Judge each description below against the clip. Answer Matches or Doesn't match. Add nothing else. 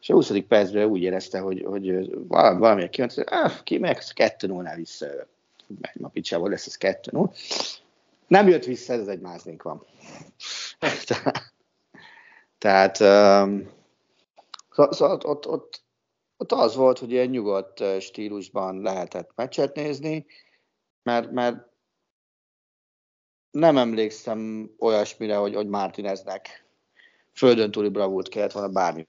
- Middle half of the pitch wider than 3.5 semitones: Matches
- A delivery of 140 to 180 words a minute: Doesn't match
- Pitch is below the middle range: Matches